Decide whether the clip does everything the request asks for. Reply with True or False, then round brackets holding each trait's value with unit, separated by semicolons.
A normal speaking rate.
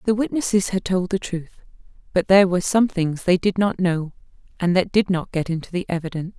False (215 wpm)